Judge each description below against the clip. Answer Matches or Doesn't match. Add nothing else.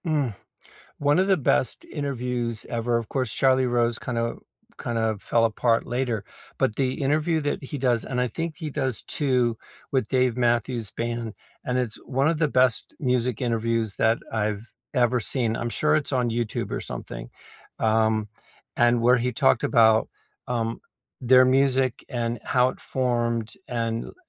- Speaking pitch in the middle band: Doesn't match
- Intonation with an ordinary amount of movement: Doesn't match